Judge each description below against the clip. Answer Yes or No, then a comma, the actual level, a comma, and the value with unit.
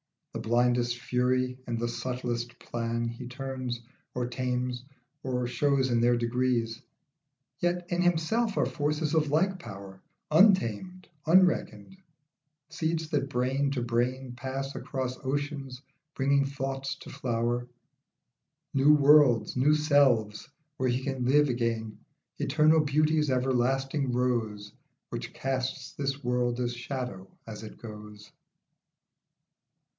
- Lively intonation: No, average, 3.0 semitones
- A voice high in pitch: No, low, 130 Hz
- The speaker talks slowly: Yes, slow, 120 wpm